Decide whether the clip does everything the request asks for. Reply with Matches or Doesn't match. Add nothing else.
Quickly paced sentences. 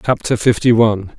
Doesn't match